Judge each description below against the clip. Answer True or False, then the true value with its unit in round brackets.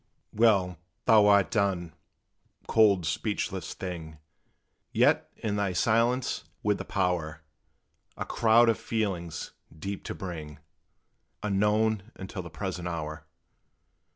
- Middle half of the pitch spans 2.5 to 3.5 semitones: False (3.9 semitones)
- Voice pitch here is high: False (95 Hz)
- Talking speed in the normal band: False (110 wpm)